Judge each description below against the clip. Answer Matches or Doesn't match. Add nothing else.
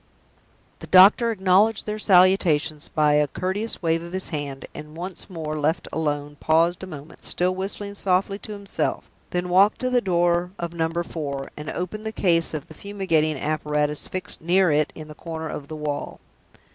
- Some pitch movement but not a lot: Matches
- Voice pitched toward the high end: Doesn't match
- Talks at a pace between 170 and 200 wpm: Matches